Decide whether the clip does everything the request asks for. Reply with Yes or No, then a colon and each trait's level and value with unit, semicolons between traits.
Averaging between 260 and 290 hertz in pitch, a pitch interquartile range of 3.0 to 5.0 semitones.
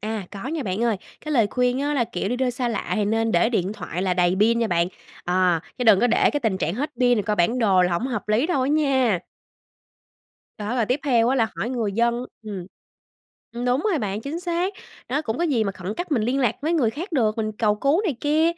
No: high, 235 Hz; average, 4.5 semitones